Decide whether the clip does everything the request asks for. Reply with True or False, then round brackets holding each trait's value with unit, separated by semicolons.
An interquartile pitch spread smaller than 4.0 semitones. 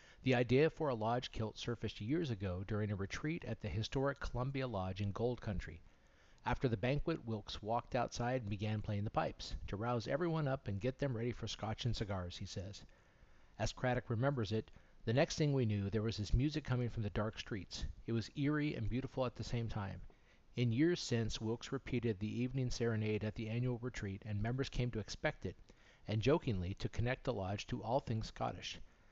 True (3.6 semitones)